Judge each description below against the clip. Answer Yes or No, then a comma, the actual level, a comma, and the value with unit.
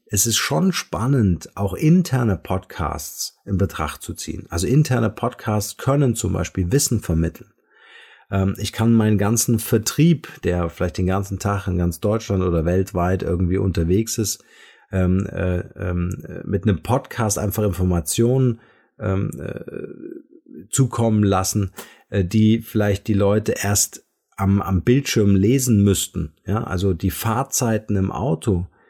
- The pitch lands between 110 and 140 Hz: No, low, 100 Hz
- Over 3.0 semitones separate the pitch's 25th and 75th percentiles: Yes, average, 3.5 semitones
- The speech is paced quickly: No, average, 140 wpm